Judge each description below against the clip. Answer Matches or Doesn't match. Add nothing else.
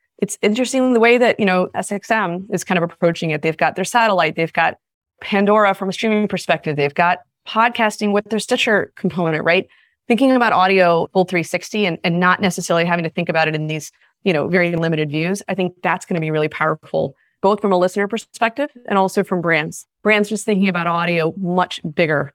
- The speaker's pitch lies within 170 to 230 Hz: Matches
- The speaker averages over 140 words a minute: Matches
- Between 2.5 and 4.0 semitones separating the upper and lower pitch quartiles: Matches